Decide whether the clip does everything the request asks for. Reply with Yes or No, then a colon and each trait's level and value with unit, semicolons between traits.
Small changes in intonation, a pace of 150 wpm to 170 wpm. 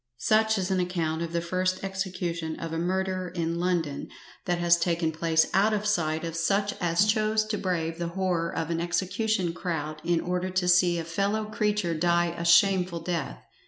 No: narrow, 2.3 semitones; average, 190 wpm